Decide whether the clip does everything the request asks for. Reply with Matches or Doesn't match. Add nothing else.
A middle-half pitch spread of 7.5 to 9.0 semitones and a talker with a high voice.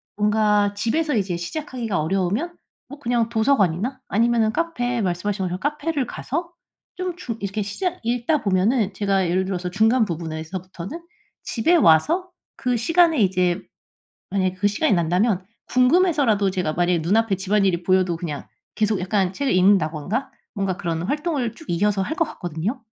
Doesn't match